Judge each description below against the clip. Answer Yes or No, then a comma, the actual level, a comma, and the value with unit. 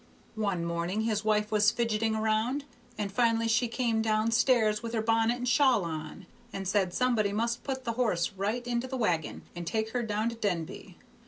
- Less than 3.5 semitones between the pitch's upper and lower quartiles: Yes, narrow, 2.6 semitones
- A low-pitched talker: No, high, 220 Hz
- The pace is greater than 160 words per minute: Yes, average, 190 wpm